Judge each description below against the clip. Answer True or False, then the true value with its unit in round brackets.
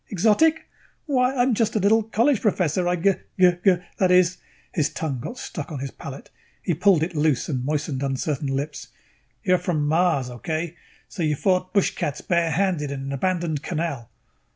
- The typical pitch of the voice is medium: True (170 Hz)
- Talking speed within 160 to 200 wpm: True (180 wpm)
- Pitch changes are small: False (4.6 semitones)